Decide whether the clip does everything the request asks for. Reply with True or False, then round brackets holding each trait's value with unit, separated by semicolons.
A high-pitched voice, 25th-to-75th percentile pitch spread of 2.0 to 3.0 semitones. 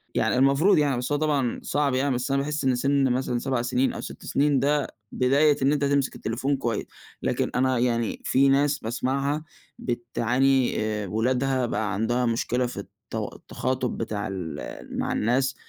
False (130 Hz; 2.5 semitones)